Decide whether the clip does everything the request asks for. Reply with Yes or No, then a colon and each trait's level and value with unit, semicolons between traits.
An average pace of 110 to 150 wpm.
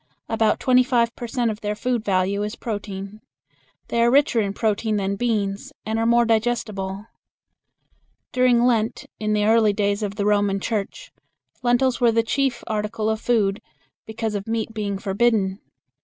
No: average, 165 wpm